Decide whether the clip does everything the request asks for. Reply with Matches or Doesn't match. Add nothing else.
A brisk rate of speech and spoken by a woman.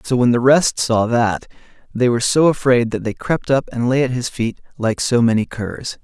Doesn't match